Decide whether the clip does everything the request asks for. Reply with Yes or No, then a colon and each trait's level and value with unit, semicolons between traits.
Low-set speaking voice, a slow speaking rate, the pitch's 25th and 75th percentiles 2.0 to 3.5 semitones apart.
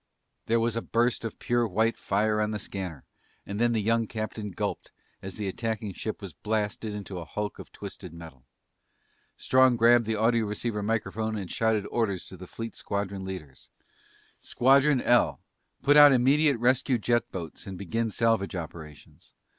No: low, 110 Hz; average, 170 wpm; average, 3.1 semitones